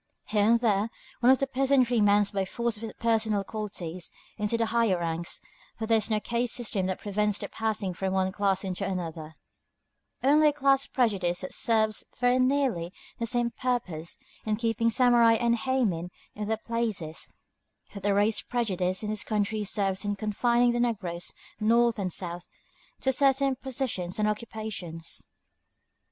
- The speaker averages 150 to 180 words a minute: Yes, average, 165 wpm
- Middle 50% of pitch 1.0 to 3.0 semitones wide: No, average, 3.7 semitones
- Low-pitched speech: No, high, 215 Hz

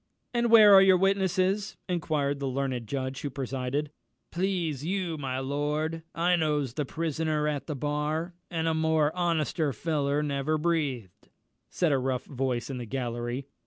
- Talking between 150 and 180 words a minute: Yes, average, 160 wpm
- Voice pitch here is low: No, medium, 150 Hz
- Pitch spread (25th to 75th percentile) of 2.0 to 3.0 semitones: No, average, 3.7 semitones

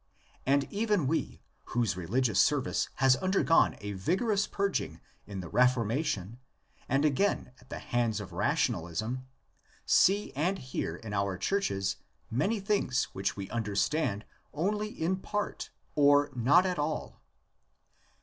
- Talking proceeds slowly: Yes, slow, 130 wpm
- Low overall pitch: Yes, low, 130 Hz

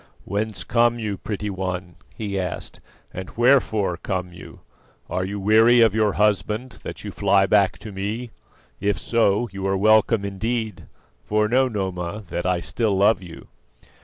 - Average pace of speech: Yes, average, 160 wpm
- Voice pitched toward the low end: Yes, low, 100 Hz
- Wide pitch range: No, average, 2.7 semitones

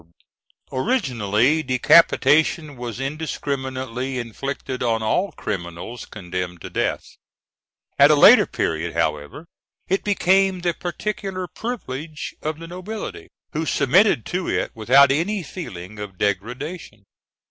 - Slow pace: Yes, slow, 115 wpm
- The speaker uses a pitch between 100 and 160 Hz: Yes, low, 135 Hz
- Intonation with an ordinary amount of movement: No, wide, 7.8 semitones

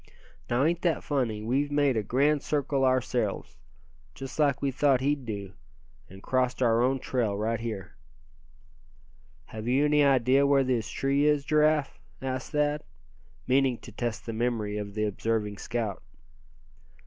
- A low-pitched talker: Yes, low, 130 Hz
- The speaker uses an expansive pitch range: No, average, 3.9 semitones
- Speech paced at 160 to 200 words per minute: No, average, 150 wpm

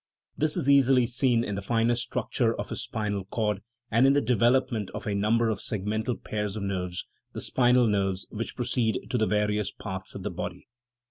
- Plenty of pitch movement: No, average, 3.2 semitones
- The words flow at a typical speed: Yes, average, 195 wpm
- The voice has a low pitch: Yes, low, 110 Hz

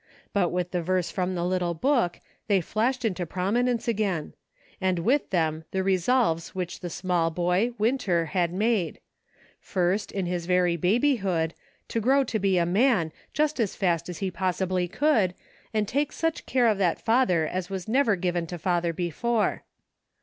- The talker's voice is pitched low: No, medium, 185 Hz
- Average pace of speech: Yes, average, 170 wpm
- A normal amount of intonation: Yes, average, 4.3 semitones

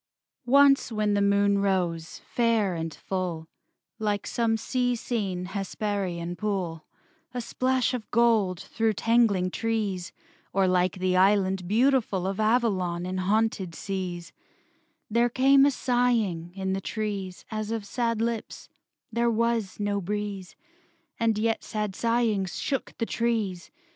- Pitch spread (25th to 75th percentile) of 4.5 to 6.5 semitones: No, average, 3.7 semitones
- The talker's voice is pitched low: No, high, 205 Hz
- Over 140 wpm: No, slow, 135 wpm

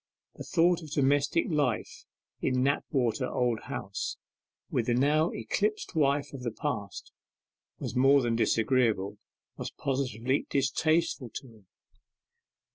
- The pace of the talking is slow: Yes, slow, 120 wpm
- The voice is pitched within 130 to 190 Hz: Yes, low, 135 Hz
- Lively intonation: No, average, 3.3 semitones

